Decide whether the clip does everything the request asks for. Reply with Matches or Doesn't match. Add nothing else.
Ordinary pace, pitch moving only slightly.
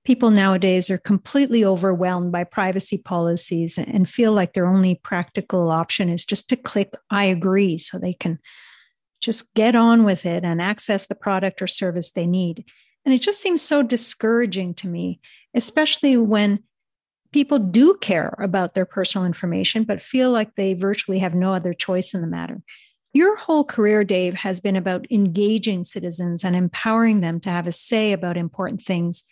Doesn't match